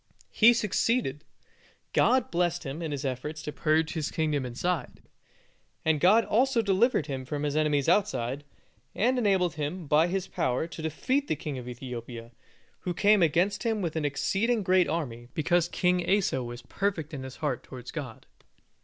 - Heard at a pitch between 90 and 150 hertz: No, medium, 160 Hz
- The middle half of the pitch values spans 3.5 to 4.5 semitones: No, wide, 5.4 semitones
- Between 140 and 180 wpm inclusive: Yes, average, 170 wpm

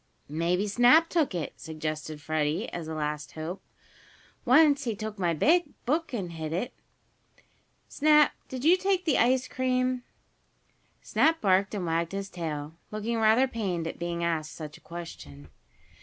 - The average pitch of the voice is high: Yes, high, 195 Hz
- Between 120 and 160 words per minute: Yes, average, 150 wpm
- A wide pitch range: Yes, wide, 8.0 semitones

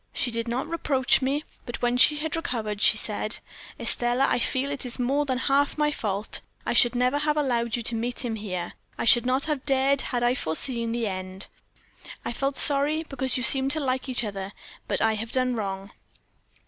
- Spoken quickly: Yes, fast, 210 wpm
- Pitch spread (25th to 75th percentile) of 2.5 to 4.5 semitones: Yes, average, 3.2 semitones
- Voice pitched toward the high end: Yes, very high, 250 Hz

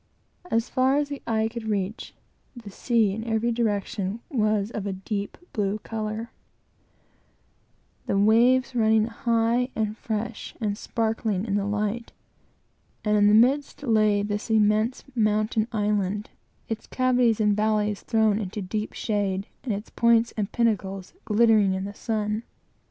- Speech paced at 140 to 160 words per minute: Yes, average, 145 wpm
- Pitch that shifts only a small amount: Yes, narrow, 1.9 semitones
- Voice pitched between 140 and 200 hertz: No, high, 215 Hz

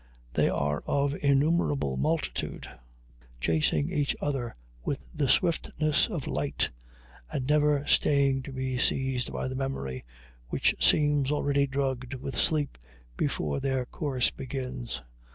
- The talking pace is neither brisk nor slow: No, slow, 125 wpm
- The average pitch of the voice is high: No, low, 135 Hz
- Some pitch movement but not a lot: No, narrow, 2.3 semitones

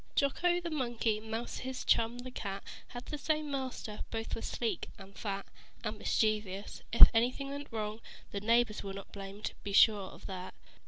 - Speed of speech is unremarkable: Yes, average, 175 wpm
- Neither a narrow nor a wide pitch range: Yes, average, 3.9 semitones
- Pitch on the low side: No, high, 225 Hz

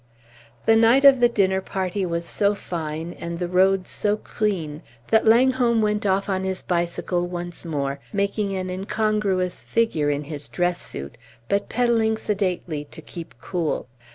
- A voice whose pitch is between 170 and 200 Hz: Yes, high, 190 Hz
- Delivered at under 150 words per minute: No, average, 155 wpm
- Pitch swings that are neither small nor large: Yes, average, 3.7 semitones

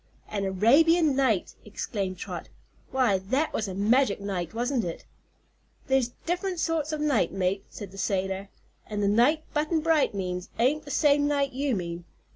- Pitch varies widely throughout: Yes, wide, 7.0 semitones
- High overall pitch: Yes, high, 235 Hz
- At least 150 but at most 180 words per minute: Yes, average, 165 wpm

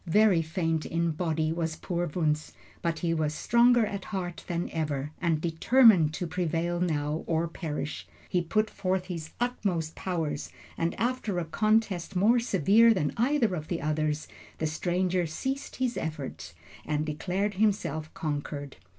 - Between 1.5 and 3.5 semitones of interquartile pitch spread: No, average, 4.1 semitones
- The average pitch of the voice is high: No, medium, 170 Hz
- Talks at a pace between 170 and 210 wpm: No, average, 150 wpm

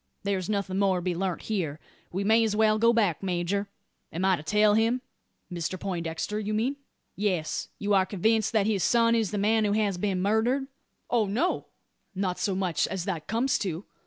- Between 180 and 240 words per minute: Yes, average, 195 wpm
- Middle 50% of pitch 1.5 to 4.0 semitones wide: Yes, average, 2.9 semitones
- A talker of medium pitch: No, high, 200 Hz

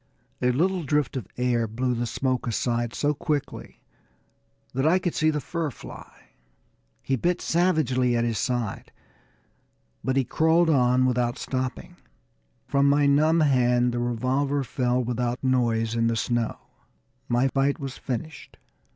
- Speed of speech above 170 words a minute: No, average, 145 wpm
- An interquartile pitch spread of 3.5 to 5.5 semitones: No, average, 3.1 semitones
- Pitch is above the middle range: No, low, 130 Hz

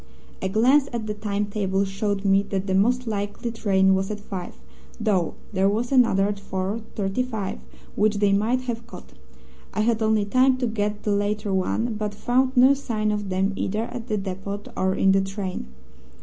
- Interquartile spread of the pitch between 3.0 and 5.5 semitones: No, narrow, 2.6 semitones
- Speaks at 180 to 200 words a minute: Yes, average, 185 wpm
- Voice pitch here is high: Yes, high, 210 Hz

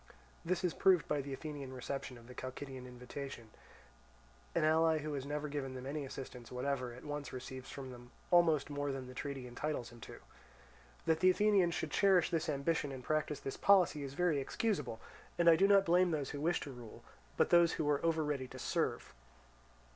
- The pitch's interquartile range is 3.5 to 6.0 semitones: Yes, average, 3.9 semitones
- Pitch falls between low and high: Yes, medium, 145 Hz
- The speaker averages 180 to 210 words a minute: Yes, average, 200 wpm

